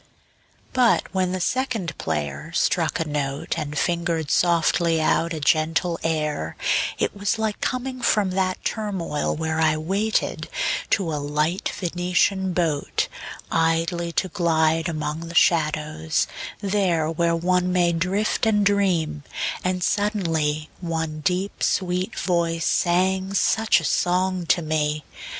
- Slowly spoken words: Yes, slow, 130 wpm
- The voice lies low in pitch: No, medium, 170 Hz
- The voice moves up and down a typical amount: Yes, average, 3.1 semitones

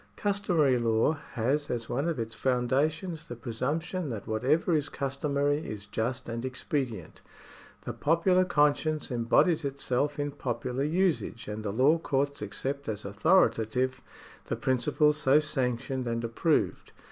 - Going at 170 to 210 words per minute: No, slow, 135 wpm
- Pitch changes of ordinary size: Yes, average, 4.4 semitones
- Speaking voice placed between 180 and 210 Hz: No, low, 135 Hz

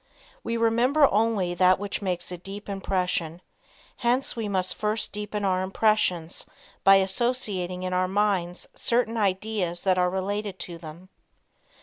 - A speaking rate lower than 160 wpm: Yes, average, 140 wpm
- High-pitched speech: Yes, high, 195 Hz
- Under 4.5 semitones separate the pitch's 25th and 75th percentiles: Yes, average, 2.8 semitones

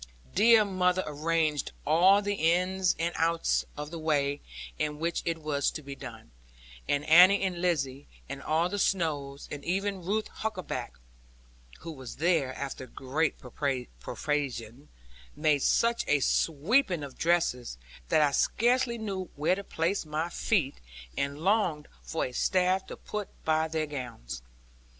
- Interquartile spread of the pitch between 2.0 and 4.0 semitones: No, average, 4.4 semitones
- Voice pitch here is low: No, medium, 160 Hz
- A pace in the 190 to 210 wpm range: No, average, 145 wpm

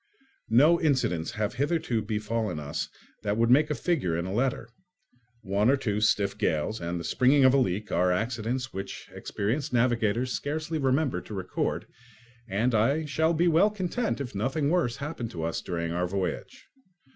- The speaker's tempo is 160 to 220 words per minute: Yes, average, 170 wpm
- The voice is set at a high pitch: No, low, 115 Hz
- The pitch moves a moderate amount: No, wide, 6.2 semitones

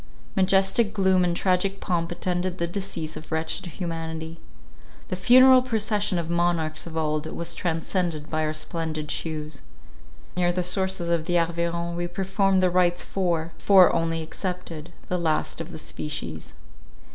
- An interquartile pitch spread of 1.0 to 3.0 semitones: Yes, narrow, 2.5 semitones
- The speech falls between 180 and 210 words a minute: No, average, 150 wpm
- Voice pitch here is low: No, medium, 175 Hz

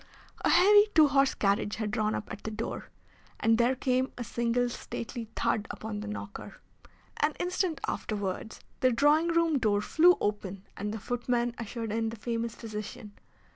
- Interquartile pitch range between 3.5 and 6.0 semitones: Yes, average, 3.9 semitones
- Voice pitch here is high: Yes, high, 230 Hz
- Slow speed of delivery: No, average, 170 wpm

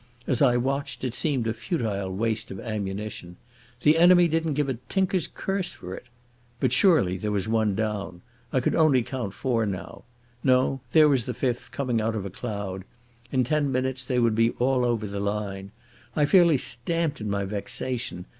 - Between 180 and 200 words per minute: Yes, average, 185 wpm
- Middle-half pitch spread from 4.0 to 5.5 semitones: Yes, average, 4.8 semitones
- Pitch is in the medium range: No, low, 120 Hz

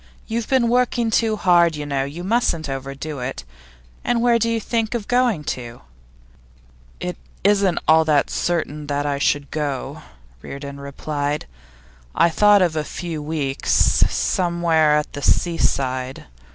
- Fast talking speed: No, average, 145 wpm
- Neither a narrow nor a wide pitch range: No, wide, 6.4 semitones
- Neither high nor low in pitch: Yes, medium, 160 Hz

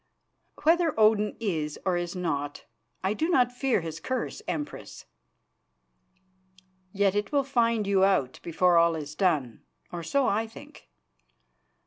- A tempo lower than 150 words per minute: Yes, slow, 135 wpm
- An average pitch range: No, wide, 6.1 semitones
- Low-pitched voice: No, high, 195 Hz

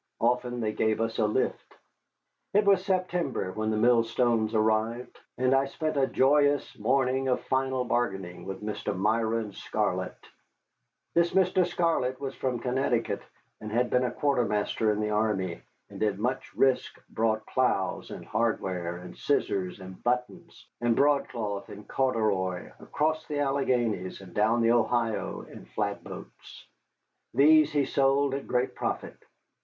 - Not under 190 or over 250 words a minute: No, average, 140 wpm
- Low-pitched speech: Yes, low, 120 Hz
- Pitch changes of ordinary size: Yes, average, 4.0 semitones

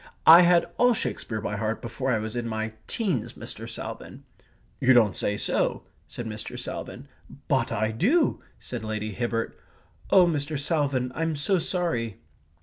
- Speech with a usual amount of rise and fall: No, wide, 6.8 semitones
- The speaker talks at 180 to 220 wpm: No, average, 155 wpm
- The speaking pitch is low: Yes, low, 125 Hz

